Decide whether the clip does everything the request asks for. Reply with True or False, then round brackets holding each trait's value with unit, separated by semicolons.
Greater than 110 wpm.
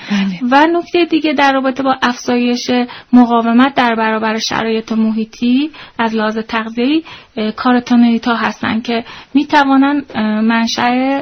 False (105 wpm)